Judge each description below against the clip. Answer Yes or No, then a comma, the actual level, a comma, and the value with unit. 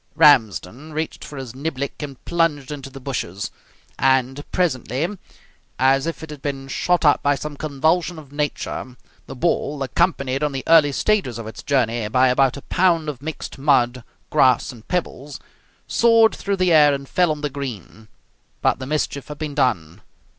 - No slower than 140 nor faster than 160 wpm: No, average, 175 wpm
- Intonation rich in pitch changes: No, average, 3.2 semitones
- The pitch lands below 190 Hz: Yes, medium, 140 Hz